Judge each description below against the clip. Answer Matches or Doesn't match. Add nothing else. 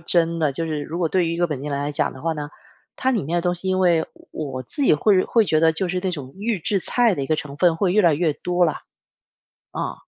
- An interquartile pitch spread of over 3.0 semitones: Matches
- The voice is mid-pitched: Matches